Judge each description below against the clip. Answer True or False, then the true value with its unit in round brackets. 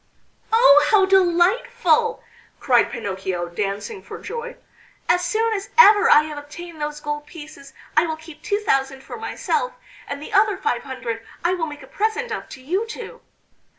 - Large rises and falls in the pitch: True (6.5 semitones)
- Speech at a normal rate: True (170 wpm)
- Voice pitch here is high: True (325 Hz)